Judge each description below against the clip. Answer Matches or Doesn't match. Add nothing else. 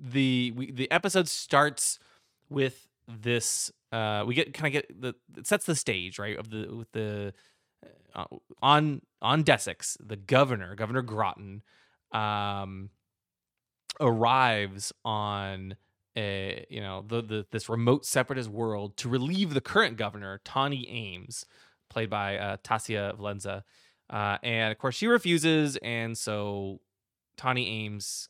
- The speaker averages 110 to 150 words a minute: Matches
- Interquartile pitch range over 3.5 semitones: Matches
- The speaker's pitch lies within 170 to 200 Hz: Doesn't match